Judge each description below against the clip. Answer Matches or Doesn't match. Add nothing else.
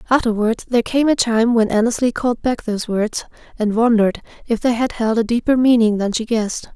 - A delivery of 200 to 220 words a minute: Matches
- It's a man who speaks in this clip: Doesn't match